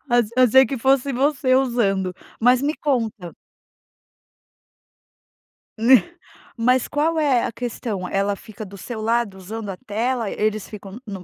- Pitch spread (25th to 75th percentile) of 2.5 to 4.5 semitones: Yes, average, 4.0 semitones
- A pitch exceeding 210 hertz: Yes, high, 230 Hz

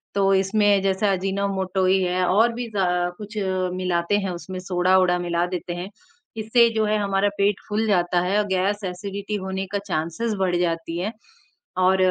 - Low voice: No, high, 190 Hz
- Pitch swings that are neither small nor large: No, narrow, 2.1 semitones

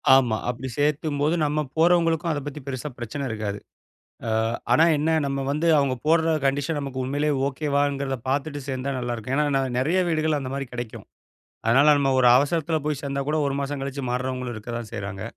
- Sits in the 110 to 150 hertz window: Yes, medium, 140 Hz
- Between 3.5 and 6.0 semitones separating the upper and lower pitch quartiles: No, average, 2.7 semitones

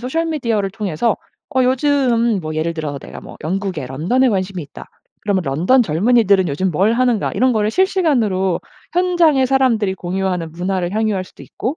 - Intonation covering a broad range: Yes, wide, 6.0 semitones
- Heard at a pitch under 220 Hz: Yes, high, 205 Hz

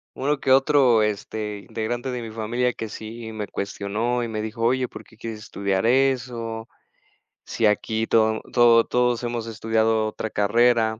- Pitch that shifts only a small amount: Yes, narrow, 1.9 semitones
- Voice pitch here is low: Yes, low, 115 Hz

